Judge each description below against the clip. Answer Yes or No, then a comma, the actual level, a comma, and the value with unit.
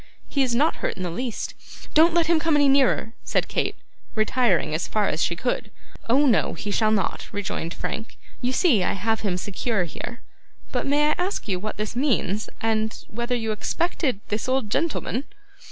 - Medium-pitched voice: No, high, 230 Hz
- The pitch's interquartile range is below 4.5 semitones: No, average, 5.0 semitones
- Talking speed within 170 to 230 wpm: Yes, average, 190 wpm